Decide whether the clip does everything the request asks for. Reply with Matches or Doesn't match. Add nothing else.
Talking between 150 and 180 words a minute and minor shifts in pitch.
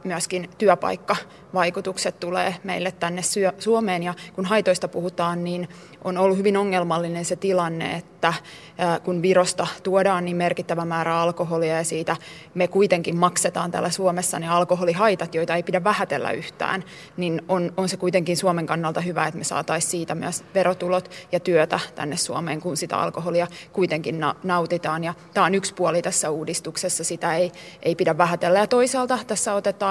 Matches